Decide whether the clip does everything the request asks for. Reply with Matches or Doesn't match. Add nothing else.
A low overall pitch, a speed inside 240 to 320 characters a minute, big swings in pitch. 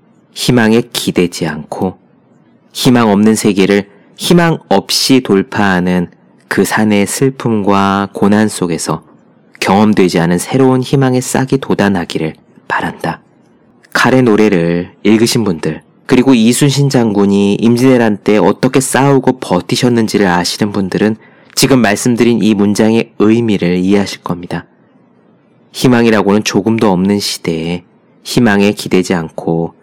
Doesn't match